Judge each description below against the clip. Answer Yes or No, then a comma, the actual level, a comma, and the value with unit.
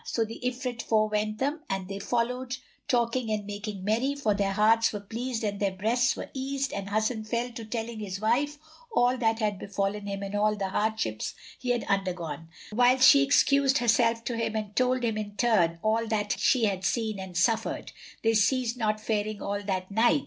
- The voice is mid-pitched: No, high, 220 Hz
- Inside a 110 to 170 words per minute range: No, average, 190 wpm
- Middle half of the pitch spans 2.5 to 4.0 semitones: Yes, average, 3.1 semitones